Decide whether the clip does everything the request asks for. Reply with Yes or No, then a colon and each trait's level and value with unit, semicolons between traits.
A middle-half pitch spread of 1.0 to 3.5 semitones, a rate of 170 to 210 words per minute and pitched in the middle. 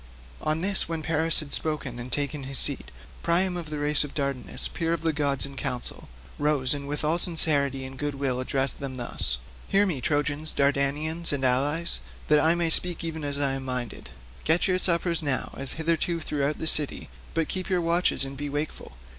Yes: average, 3.1 semitones; average, 195 wpm; medium, 150 Hz